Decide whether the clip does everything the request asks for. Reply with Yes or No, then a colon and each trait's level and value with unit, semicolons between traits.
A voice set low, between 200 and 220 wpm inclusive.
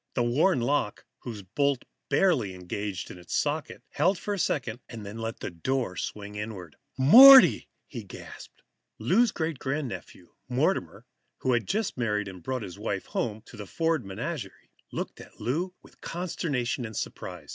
No: low, 120 Hz; average, 155 wpm